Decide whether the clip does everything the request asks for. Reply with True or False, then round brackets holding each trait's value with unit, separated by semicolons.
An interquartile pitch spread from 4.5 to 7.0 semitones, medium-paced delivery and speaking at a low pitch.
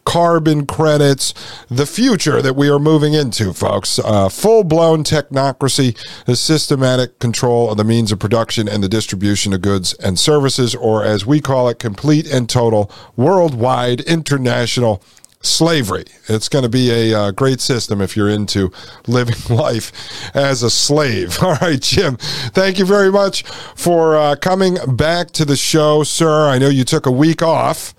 True (5.1 semitones; 165 wpm; 130 Hz)